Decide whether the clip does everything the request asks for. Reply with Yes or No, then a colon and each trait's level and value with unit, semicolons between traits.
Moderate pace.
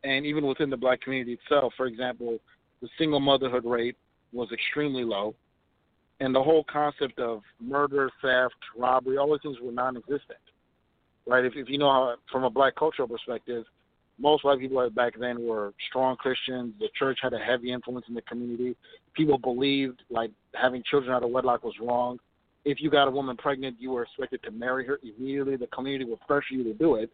Yes: average, 190 wpm